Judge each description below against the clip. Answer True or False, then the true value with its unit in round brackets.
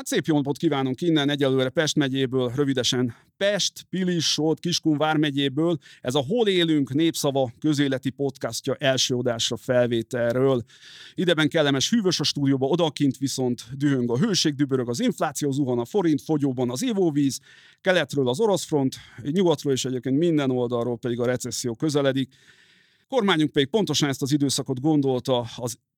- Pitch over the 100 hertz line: True (140 Hz)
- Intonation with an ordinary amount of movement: True (3.5 semitones)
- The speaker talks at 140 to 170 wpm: True (150 wpm)